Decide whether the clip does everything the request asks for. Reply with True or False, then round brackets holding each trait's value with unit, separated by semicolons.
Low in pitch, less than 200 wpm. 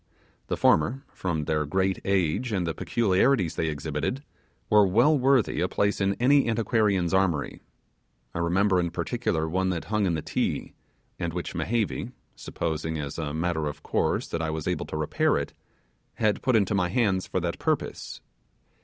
True (95 Hz; 170 wpm)